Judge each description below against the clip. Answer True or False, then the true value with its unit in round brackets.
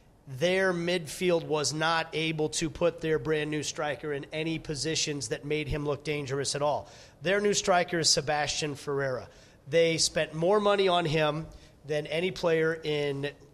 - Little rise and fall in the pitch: True (2.1 semitones)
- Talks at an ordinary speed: True (165 wpm)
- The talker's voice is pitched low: False (155 Hz)